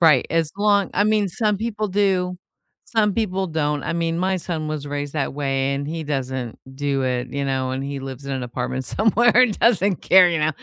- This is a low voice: No, medium, 155 Hz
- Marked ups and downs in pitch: Yes, wide, 6.0 semitones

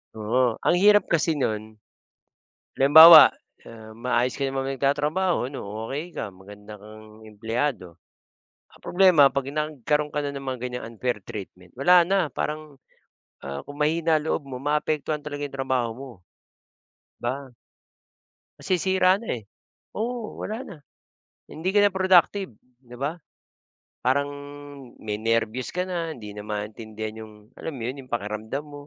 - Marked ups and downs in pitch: Yes, wide, 6.1 semitones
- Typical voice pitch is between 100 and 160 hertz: Yes, low, 135 Hz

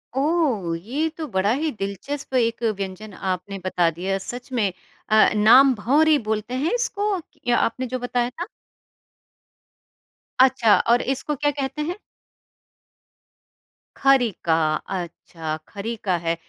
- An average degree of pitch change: No, wide, 6.0 semitones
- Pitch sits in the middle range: No, high, 235 Hz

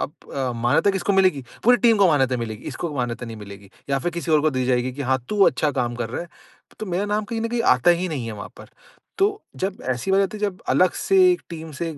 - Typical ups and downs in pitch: No, wide, 7.6 semitones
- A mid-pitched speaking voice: Yes, medium, 155 Hz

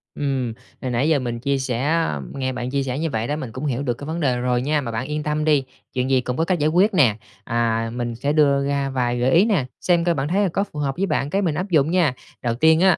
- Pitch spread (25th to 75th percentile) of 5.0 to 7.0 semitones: No, average, 4.2 semitones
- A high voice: No, medium, 140 Hz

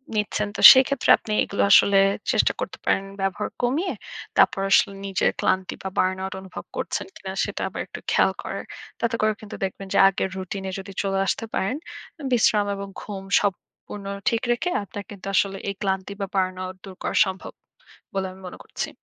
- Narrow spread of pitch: Yes, narrow, 1.6 semitones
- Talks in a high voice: Yes, high, 195 Hz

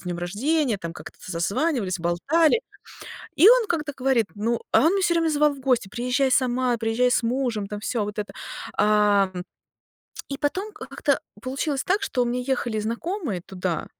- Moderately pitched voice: No, high, 245 Hz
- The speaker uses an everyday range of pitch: No, wide, 5.9 semitones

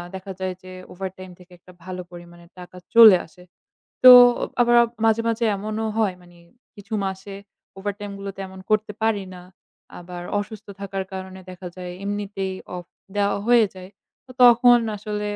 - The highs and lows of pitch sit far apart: No, narrow, 2.5 semitones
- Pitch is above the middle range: Yes, high, 195 Hz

